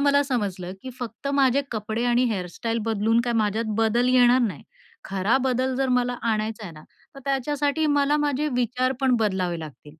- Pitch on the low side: No, high, 240 Hz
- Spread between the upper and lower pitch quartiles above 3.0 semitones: Yes, average, 3.5 semitones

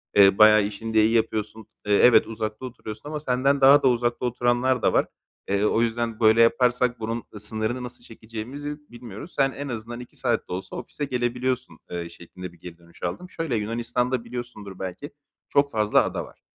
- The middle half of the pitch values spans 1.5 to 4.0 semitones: Yes, average, 2.7 semitones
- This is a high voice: No, low, 115 Hz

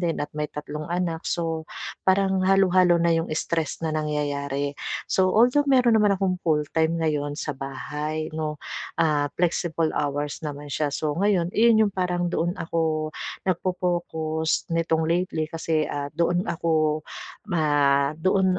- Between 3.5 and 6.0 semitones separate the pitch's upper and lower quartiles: No, average, 3.0 semitones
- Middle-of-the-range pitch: Yes, medium, 160 Hz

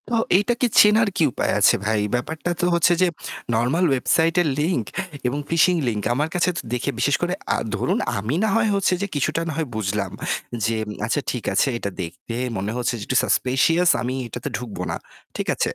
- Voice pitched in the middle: Yes, medium, 145 Hz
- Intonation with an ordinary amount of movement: No, wide, 7.2 semitones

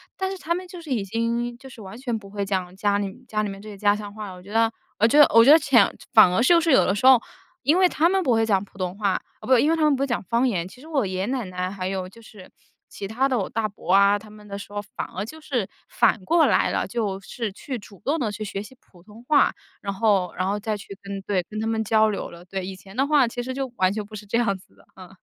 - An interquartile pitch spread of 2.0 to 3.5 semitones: No, average, 4.3 semitones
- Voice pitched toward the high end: Yes, high, 215 Hz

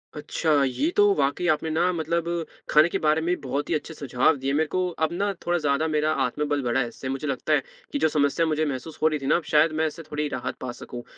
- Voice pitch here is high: No, medium, 150 Hz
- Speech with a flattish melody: No, average, 3.0 semitones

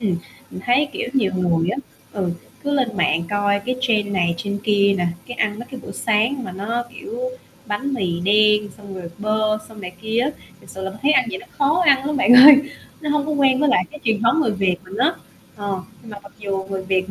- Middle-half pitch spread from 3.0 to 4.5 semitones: No, average, 5.1 semitones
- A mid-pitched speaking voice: No, high, 215 Hz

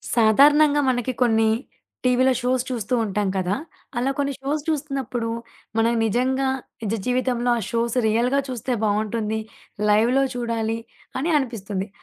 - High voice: Yes, high, 240 Hz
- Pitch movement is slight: No, average, 3.1 semitones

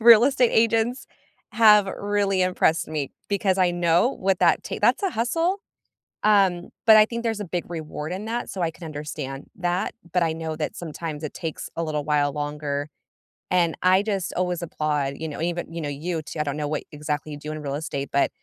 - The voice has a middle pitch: Yes, medium, 170 Hz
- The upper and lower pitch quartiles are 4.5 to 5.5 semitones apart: Yes, average, 5.0 semitones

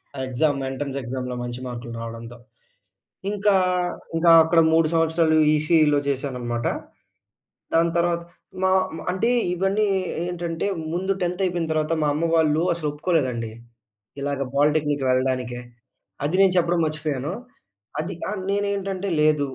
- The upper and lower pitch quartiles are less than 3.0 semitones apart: No, average, 4.5 semitones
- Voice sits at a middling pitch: Yes, medium, 155 Hz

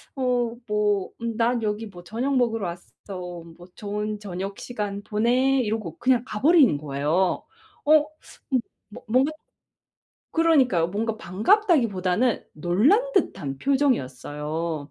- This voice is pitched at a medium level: No, high, 215 Hz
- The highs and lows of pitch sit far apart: Yes, wide, 6.1 semitones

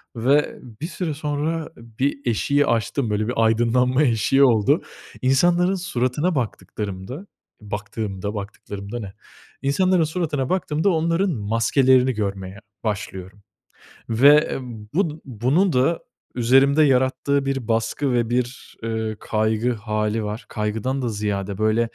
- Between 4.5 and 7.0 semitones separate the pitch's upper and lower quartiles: Yes, average, 5.0 semitones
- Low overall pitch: Yes, low, 125 Hz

